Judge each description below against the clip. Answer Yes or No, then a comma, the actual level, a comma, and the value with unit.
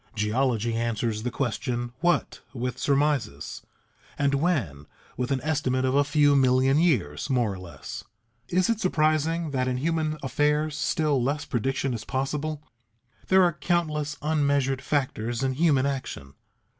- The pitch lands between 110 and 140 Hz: Yes, low, 135 Hz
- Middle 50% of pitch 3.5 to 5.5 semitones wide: Yes, average, 3.9 semitones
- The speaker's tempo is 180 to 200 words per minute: No, average, 145 wpm